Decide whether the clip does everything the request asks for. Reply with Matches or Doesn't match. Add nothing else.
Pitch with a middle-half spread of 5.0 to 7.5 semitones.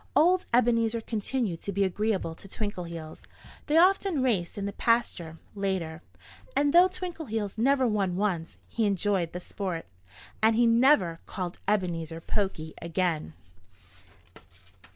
Matches